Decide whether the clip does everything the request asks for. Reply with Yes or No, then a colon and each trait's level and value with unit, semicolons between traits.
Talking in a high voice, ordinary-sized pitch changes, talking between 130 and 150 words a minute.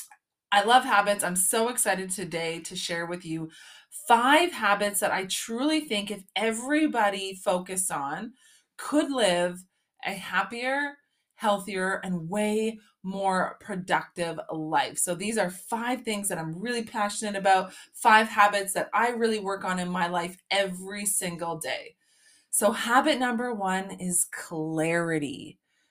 Yes: high, 200 Hz; average, 4.1 semitones; average, 140 wpm